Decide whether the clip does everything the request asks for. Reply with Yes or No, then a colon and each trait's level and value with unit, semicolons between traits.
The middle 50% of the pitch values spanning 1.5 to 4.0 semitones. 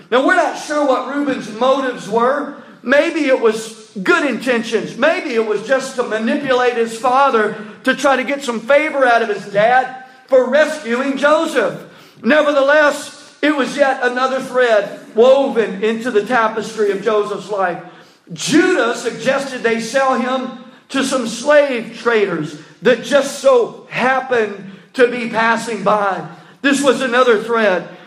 Yes: average, 3.6 semitones